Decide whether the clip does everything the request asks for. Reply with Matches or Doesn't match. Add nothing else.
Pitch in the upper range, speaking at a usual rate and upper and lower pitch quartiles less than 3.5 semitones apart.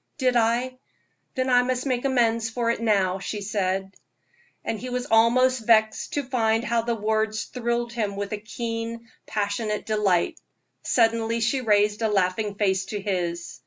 Matches